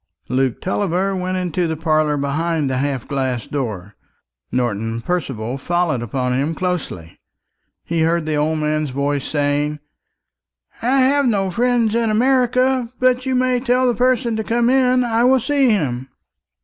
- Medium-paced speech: Yes, average, 155 wpm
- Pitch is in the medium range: Yes, medium, 170 Hz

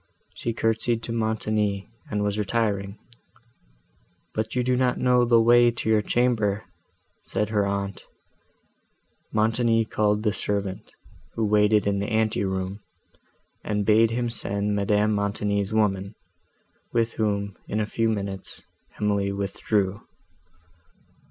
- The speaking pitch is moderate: No, low, 105 Hz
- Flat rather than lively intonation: Yes, narrow, 2.0 semitones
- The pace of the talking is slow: Yes, slow, 125 wpm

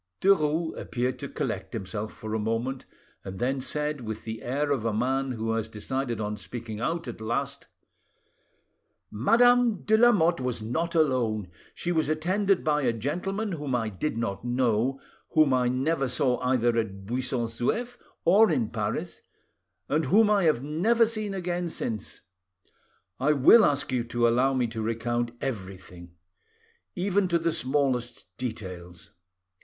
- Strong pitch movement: Yes, wide, 6.3 semitones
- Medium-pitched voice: No, low, 130 Hz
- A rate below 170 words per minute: Yes, average, 155 wpm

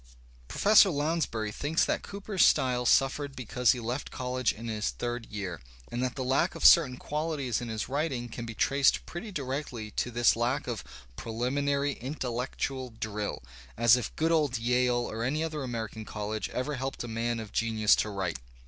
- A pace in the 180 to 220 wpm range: Yes, average, 185 wpm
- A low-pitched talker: Yes, low, 125 Hz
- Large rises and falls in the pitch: No, average, 3.8 semitones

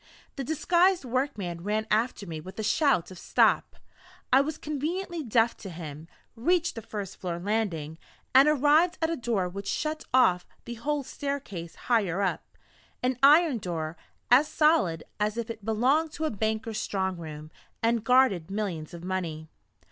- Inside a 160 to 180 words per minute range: Yes, average, 165 wpm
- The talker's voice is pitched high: Yes, high, 225 Hz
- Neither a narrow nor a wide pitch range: No, wide, 7.6 semitones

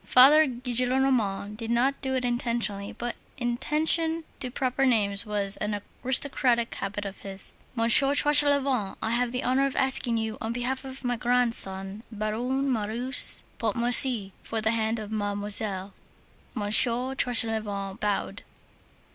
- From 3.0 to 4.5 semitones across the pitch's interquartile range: Yes, average, 3.7 semitones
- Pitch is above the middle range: Yes, high, 235 Hz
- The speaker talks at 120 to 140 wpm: Yes, slow, 135 wpm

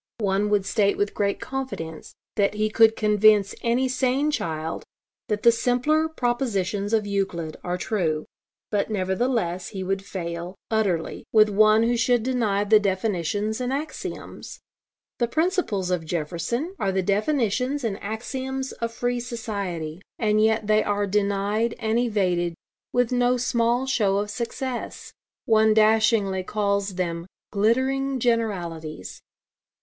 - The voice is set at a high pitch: Yes, high, 215 Hz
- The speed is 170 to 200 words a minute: No, slow, 135 wpm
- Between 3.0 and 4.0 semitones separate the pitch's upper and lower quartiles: Yes, average, 3.7 semitones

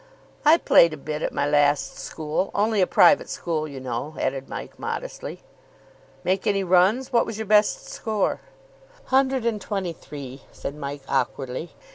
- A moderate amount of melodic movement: No, wide, 7.1 semitones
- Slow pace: No, average, 160 wpm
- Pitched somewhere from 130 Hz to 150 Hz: No, medium, 175 Hz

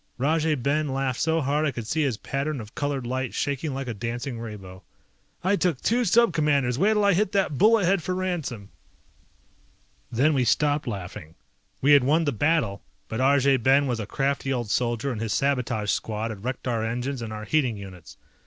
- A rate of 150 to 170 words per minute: No, average, 195 wpm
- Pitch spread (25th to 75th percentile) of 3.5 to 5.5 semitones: Yes, average, 4.9 semitones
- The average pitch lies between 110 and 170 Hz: Yes, low, 135 Hz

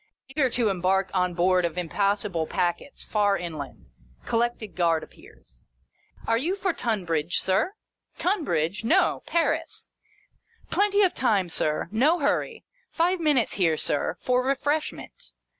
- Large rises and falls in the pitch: Yes, wide, 8.6 semitones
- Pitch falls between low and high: No, high, 210 Hz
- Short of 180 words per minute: Yes, average, 145 wpm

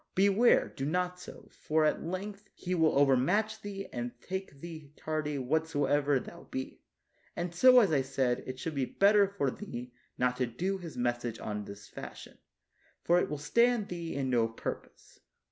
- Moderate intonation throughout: No, wide, 6.5 semitones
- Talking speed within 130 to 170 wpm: No, average, 180 wpm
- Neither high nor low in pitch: Yes, medium, 155 Hz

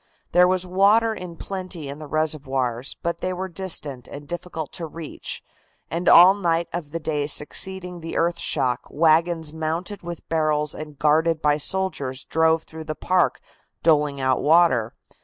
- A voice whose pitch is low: No, medium, 160 Hz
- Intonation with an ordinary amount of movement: Yes, average, 3.0 semitones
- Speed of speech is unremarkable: Yes, average, 160 wpm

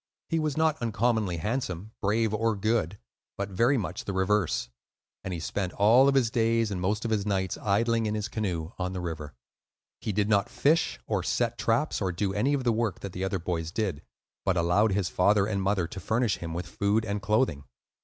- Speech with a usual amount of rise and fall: Yes, average, 3.6 semitones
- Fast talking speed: Yes, fast, 210 wpm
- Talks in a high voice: No, low, 105 Hz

